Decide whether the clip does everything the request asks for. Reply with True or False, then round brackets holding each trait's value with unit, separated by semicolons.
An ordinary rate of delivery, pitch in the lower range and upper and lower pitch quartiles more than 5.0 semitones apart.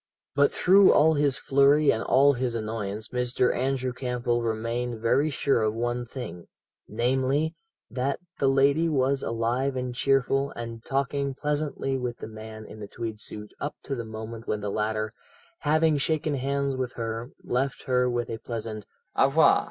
False (165 wpm; 125 Hz; 3.4 semitones)